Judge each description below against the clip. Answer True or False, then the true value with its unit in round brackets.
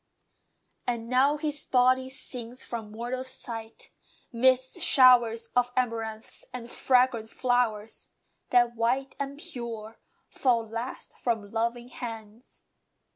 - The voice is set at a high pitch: True (245 Hz)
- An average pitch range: False (2.2 semitones)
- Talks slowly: True (110 wpm)